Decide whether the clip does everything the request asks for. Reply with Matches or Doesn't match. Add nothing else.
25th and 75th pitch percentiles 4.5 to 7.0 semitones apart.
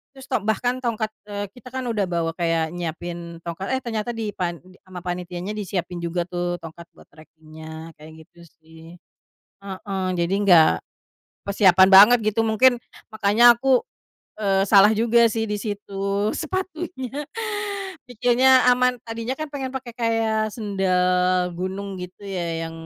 Matches